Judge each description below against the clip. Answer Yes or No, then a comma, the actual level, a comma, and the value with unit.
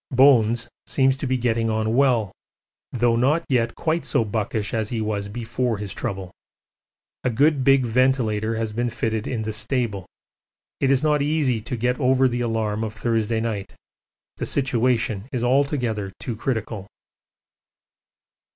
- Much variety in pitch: No, average, 2.8 semitones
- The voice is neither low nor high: No, low, 115 Hz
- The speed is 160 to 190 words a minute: No, average, 150 wpm